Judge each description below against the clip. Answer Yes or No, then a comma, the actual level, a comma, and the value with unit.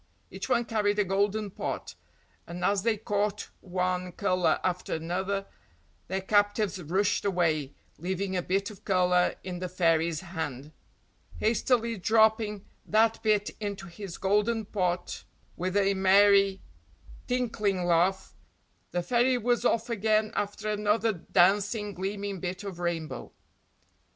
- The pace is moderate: No, slow, 130 wpm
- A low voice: No, high, 195 Hz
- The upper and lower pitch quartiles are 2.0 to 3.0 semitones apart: Yes, average, 2.7 semitones